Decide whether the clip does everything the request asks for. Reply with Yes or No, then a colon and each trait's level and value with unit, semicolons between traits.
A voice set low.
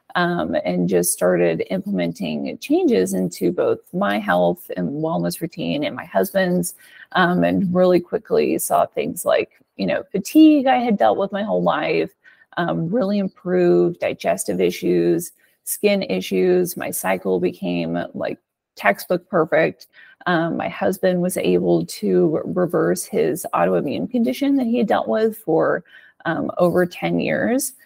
No: medium, 180 Hz